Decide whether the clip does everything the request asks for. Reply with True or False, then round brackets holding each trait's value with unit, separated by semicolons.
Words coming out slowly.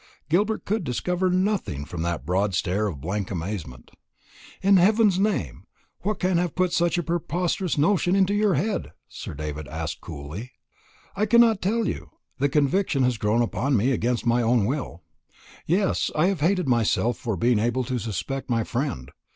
False (170 wpm)